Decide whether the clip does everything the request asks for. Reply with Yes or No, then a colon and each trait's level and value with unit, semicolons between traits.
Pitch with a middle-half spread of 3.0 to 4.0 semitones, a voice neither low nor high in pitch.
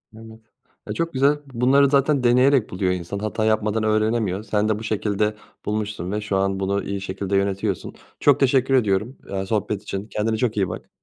No: average, 3.4 semitones; low, 110 Hz